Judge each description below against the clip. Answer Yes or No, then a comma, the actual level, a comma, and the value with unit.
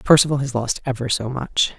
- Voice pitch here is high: No, low, 130 Hz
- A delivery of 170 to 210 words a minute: Yes, average, 200 wpm